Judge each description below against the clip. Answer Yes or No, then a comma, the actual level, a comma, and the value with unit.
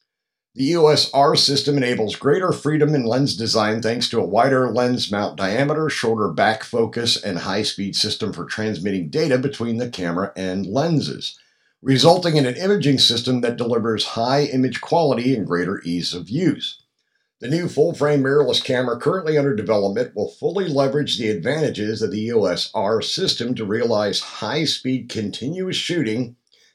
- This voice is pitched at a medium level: No, low, 125 Hz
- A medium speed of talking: Yes, average, 150 wpm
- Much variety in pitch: No, average, 4.9 semitones